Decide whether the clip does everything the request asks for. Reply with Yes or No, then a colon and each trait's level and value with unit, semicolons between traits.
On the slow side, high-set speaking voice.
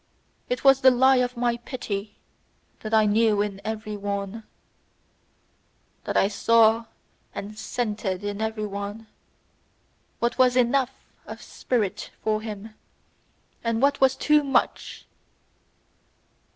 Yes: slow, 120 wpm; high, 220 Hz